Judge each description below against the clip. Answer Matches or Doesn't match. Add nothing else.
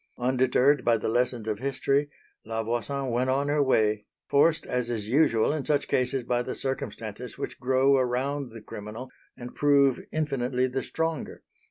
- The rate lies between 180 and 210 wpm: Doesn't match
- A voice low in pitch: Matches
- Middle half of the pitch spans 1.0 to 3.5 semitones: Matches